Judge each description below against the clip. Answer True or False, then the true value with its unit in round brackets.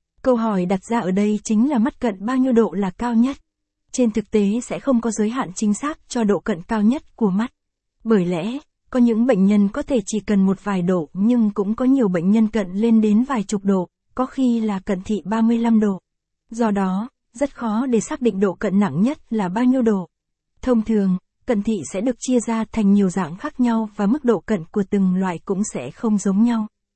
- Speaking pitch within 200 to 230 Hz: True (220 Hz)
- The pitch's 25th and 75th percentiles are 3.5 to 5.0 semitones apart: False (2.8 semitones)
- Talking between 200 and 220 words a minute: False (235 wpm)